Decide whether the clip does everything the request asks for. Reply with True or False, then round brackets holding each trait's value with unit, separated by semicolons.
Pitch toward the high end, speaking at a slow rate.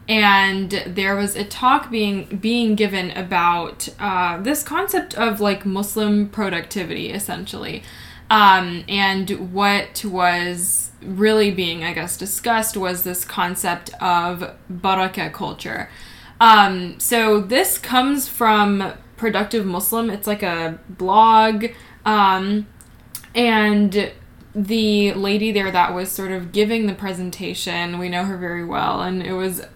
True (195 Hz; 125 wpm)